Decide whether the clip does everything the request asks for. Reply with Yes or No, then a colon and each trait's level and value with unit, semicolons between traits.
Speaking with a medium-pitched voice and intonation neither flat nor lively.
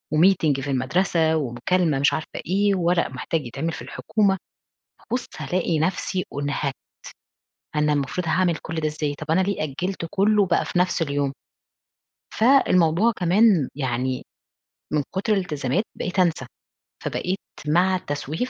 Yes: medium, 165 Hz; average, 4.4 semitones